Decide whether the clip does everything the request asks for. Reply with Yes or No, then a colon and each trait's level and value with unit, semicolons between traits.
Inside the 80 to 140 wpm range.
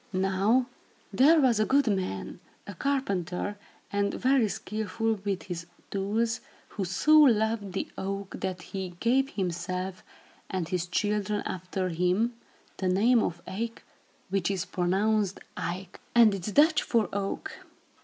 Yes: slow, 135 wpm